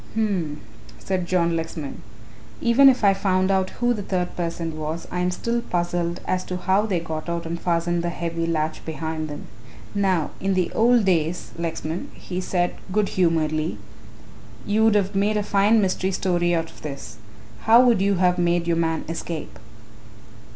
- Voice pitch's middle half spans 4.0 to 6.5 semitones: No, average, 2.8 semitones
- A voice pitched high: No, medium, 175 Hz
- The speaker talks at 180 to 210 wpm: No, average, 170 wpm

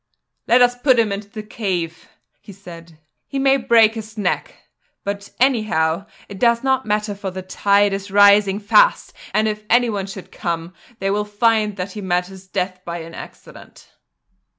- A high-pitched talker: Yes, high, 205 Hz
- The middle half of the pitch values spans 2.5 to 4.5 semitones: Yes, average, 2.8 semitones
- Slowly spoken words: No, average, 175 wpm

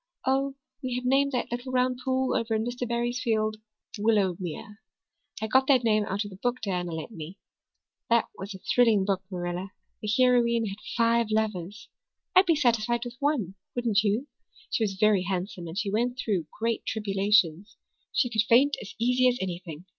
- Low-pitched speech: No, high, 220 Hz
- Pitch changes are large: No, average, 3.9 semitones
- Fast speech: No, average, 180 wpm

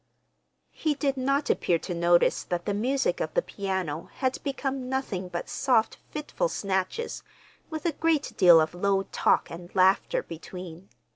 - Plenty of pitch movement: Yes, wide, 7.6 semitones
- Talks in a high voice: Yes, high, 200 Hz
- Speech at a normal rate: Yes, average, 155 wpm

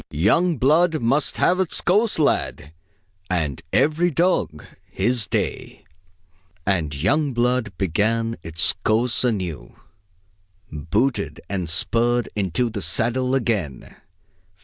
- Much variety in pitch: Yes, wide, 7.2 semitones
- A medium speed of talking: No, slow, 105 wpm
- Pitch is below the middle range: Yes, low, 115 Hz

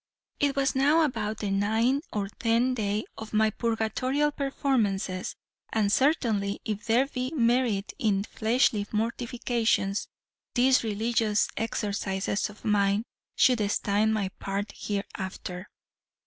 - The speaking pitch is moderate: No, high, 220 Hz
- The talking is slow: Yes, slow, 120 wpm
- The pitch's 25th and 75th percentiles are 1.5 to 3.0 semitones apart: No, average, 3.7 semitones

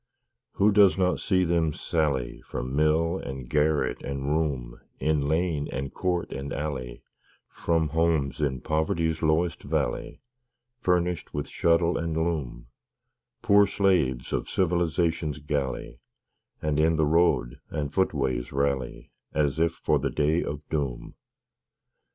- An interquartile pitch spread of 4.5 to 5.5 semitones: No, average, 3.2 semitones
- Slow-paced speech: Yes, slow, 130 wpm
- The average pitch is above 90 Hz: No, very low, 80 Hz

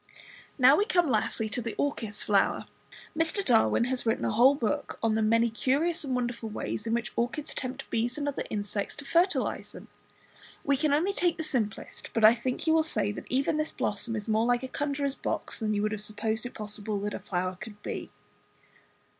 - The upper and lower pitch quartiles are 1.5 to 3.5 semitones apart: No, average, 4.7 semitones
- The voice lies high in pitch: Yes, high, 240 Hz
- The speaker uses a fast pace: Yes, fast, 210 wpm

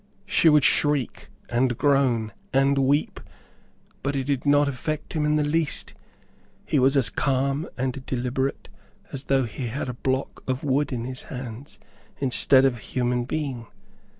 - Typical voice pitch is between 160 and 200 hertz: No, low, 135 Hz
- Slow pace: No, average, 160 wpm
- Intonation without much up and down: Yes, narrow, 2.1 semitones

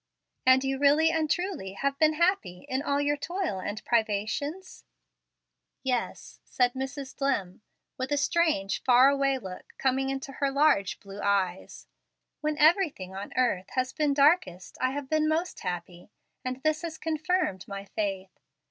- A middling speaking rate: Yes, average, 155 wpm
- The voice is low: No, very high, 270 Hz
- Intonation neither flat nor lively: No, wide, 7.3 semitones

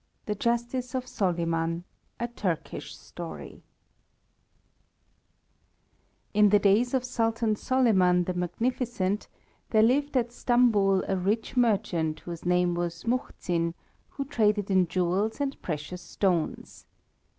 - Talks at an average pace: No, slow, 115 wpm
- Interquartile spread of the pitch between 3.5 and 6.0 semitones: Yes, average, 5.1 semitones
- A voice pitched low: No, high, 205 Hz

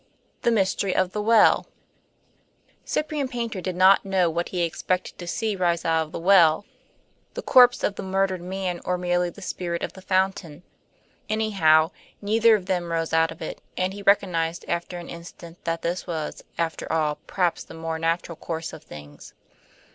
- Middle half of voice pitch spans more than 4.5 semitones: No, average, 2.8 semitones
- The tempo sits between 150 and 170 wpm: No, average, 180 wpm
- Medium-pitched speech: Yes, medium, 180 Hz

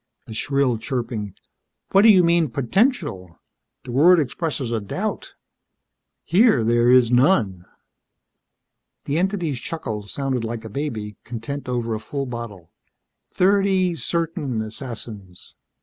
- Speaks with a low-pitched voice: Yes, low, 125 Hz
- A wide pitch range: Yes, wide, 6.7 semitones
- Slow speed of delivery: Yes, slow, 120 wpm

